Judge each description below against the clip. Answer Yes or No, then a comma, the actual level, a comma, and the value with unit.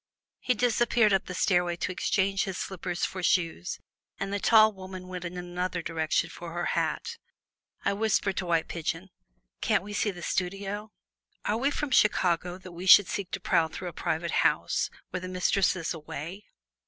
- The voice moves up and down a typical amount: No, narrow, 2.3 semitones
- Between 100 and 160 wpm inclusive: No, average, 180 wpm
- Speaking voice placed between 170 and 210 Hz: Yes, medium, 185 Hz